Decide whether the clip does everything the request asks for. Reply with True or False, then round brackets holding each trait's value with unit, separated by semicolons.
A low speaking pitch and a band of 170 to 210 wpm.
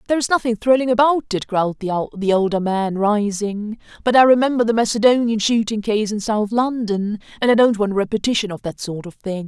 False (220 Hz; 205 wpm)